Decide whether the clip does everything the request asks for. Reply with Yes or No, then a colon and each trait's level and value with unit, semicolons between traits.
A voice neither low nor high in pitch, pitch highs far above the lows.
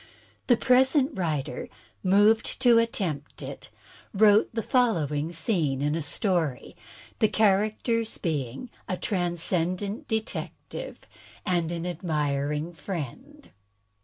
Yes: medium, 180 Hz; wide, 6.0 semitones